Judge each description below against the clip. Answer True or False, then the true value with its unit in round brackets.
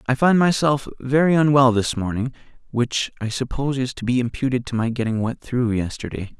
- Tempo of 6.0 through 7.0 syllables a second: False (5.5 syllables/s)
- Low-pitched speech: True (125 Hz)